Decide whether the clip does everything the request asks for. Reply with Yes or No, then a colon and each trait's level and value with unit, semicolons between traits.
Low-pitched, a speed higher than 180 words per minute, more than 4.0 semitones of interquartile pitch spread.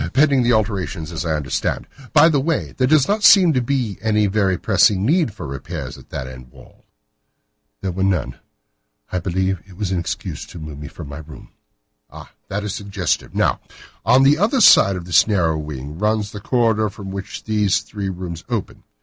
Yes: low, 100 Hz; average, 200 wpm; average, 5.2 semitones